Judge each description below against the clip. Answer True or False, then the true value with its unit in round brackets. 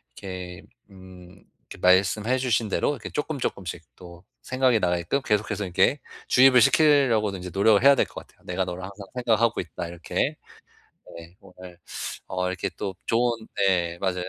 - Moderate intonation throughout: True (4.5 semitones)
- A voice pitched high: False (100 Hz)